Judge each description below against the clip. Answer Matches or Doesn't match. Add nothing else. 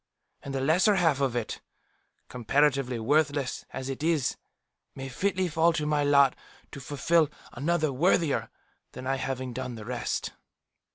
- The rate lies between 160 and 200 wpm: Doesn't match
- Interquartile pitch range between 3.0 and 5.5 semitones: Matches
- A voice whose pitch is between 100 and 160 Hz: Matches